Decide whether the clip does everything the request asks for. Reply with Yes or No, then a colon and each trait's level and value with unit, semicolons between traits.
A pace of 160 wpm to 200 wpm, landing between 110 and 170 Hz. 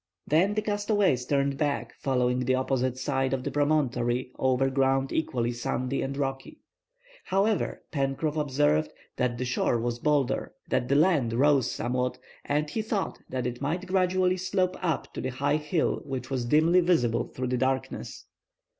Yes: average, 165 wpm; low, 135 Hz